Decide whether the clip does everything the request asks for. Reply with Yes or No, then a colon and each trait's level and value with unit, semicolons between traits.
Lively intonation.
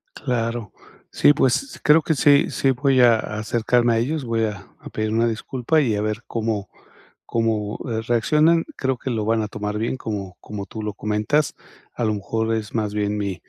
No: average, 3.3 semitones